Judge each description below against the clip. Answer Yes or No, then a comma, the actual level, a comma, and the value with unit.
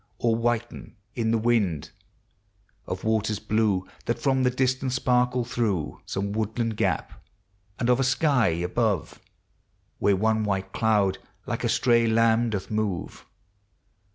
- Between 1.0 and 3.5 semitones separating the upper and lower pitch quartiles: Yes, average, 2.9 semitones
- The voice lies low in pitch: Yes, low, 110 Hz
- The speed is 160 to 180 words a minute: No, slow, 135 wpm